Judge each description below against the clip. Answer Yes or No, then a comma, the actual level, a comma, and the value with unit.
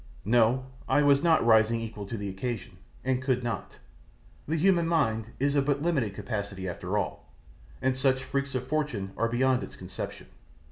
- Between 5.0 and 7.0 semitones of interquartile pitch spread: No, average, 4.2 semitones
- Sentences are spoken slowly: No, average, 175 wpm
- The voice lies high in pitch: No, low, 125 Hz